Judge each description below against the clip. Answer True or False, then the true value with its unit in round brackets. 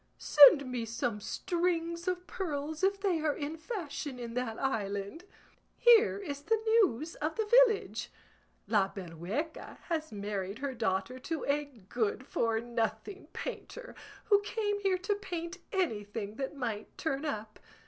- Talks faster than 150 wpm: False (145 wpm)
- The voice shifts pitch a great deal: True (8.3 semitones)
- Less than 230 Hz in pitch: False (290 Hz)